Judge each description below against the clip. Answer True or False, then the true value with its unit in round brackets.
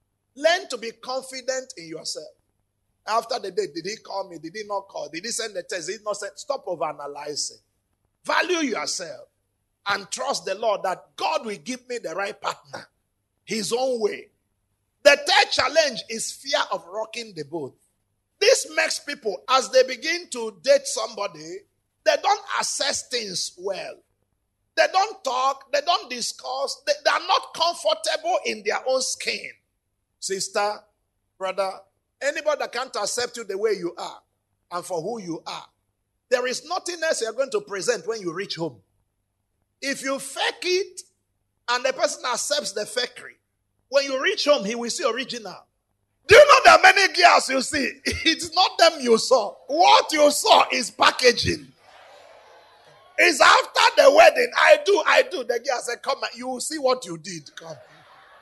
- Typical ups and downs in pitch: False (7.8 semitones)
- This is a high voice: True (265 Hz)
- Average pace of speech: True (175 wpm)